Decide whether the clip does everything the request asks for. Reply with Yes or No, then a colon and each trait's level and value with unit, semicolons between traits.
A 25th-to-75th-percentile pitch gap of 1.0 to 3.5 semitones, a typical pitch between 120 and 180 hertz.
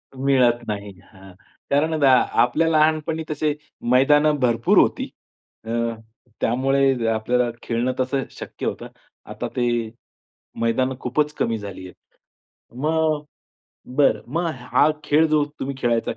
No: average, 4.2 semitones; low, 135 Hz